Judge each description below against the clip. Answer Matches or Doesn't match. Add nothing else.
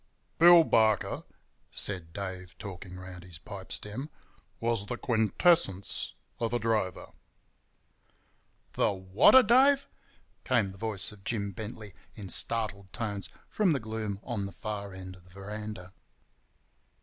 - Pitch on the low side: Matches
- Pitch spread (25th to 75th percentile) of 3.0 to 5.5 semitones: Matches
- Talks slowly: Matches